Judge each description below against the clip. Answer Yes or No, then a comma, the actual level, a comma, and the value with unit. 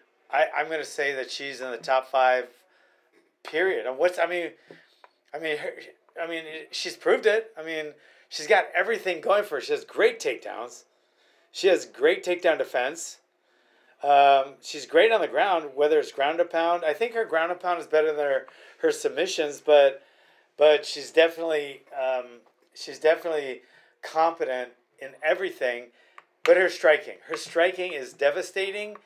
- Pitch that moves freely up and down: Yes, wide, 7.1 semitones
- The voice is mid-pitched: Yes, medium, 165 Hz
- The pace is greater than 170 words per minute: No, average, 165 wpm